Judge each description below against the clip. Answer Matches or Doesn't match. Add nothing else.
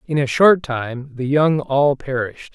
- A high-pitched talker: Doesn't match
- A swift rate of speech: Doesn't match